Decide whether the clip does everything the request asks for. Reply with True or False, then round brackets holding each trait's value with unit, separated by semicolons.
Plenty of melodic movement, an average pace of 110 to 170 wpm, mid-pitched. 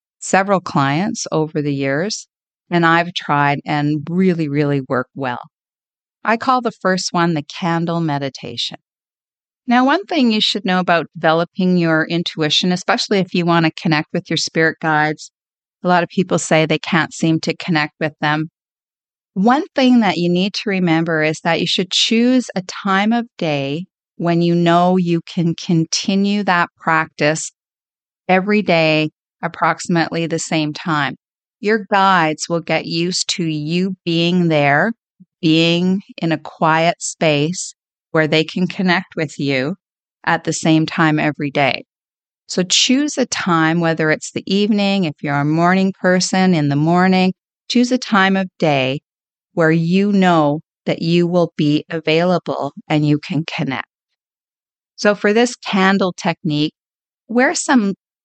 False (3.4 semitones; 155 wpm; 170 Hz)